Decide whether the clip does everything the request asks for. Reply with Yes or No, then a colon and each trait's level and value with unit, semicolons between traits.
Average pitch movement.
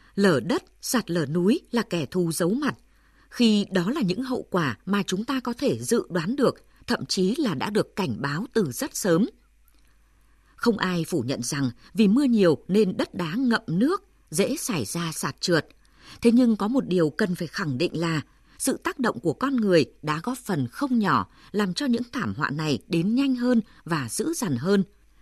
No: wide, 6.3 semitones